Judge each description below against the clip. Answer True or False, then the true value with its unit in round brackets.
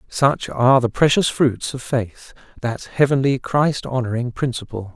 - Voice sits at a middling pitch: False (125 Hz)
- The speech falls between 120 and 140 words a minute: True (135 wpm)